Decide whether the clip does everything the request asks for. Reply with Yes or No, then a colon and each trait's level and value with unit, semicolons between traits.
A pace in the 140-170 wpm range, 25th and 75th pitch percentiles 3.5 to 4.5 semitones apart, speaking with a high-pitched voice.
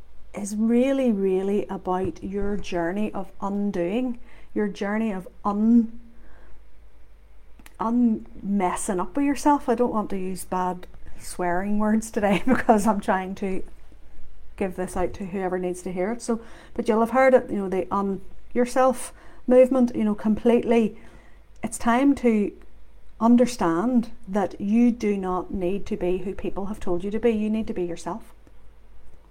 Yes: average, 160 wpm; average, 4.0 semitones; high, 205 Hz